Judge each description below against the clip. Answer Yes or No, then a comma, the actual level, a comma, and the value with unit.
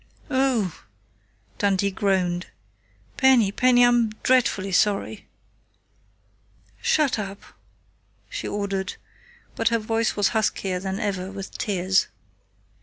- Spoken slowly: Yes, slow, 100 wpm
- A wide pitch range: No, average, 3.2 semitones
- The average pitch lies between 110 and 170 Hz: No, high, 205 Hz